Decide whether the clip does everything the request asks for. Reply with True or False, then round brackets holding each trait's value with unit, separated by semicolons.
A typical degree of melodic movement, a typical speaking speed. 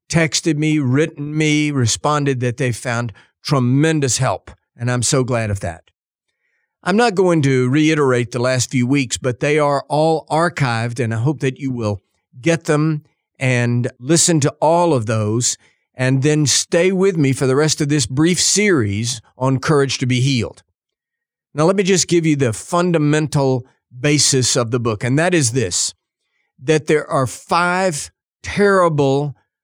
True (4.0 semitones; 165 wpm)